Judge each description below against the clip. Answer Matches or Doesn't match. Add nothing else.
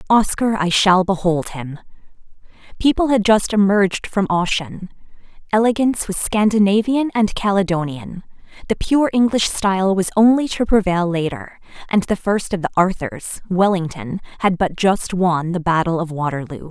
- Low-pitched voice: Doesn't match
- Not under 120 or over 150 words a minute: Matches